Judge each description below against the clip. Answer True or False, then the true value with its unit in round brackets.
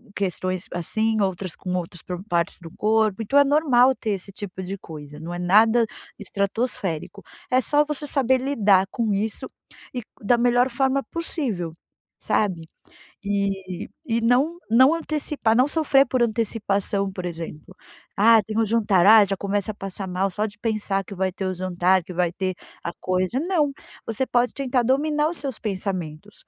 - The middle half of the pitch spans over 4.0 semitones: True (5.0 semitones)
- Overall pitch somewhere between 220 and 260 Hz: False (210 Hz)